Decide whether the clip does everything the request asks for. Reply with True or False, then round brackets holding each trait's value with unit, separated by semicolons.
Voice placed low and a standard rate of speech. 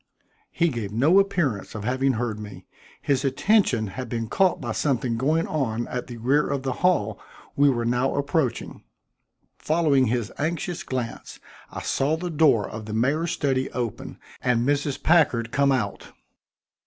True (130 Hz; 160 wpm)